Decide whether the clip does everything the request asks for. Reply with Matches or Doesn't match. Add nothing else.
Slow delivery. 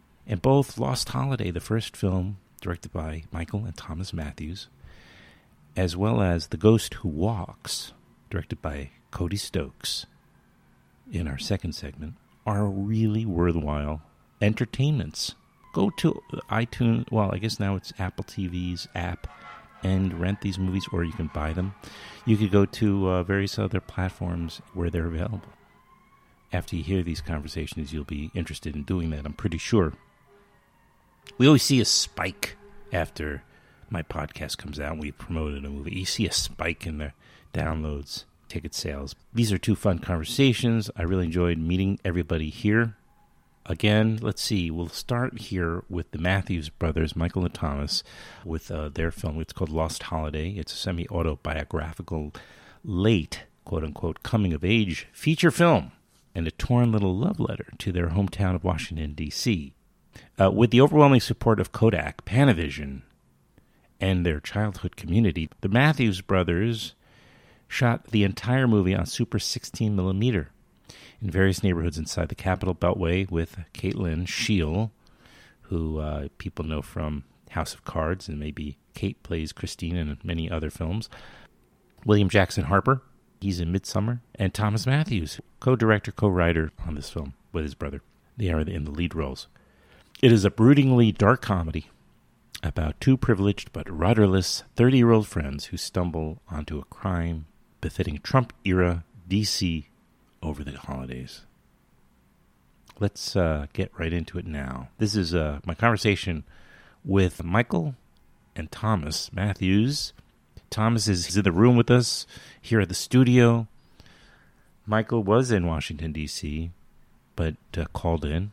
Doesn't match